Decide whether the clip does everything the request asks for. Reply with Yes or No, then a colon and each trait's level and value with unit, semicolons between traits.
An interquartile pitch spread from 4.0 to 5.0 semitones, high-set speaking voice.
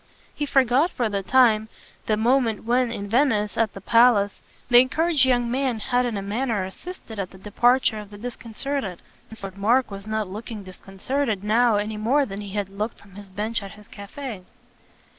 No: average, 3.6 semitones; high, 220 Hz